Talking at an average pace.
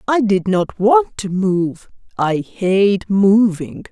No: slow, 125 wpm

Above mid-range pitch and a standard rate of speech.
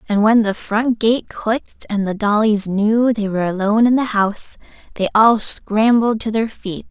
Yes: high, 215 Hz; average, 190 wpm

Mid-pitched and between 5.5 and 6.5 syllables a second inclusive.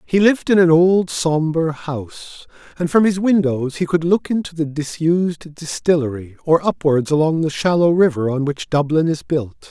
No: medium, 160 Hz; 4.8 syllables/s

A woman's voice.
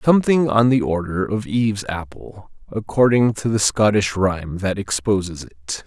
No: male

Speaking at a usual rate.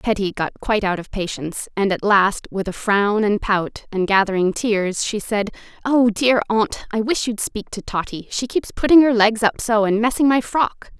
No: fast, 215 wpm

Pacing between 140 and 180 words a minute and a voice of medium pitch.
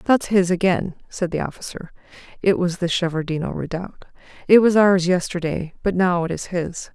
Yes: average, 175 wpm; medium, 180 Hz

